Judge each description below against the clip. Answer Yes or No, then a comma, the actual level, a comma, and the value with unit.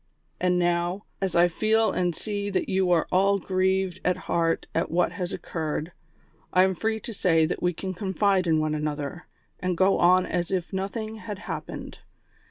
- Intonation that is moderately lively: No, narrow, 2.2 semitones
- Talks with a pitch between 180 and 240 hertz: Yes, medium, 185 Hz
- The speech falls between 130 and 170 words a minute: No, average, 190 wpm